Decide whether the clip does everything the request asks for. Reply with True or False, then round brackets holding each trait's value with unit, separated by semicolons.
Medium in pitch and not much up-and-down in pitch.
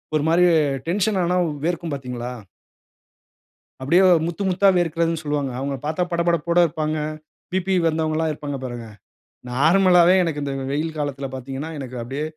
False (155 Hz; 3.7 semitones)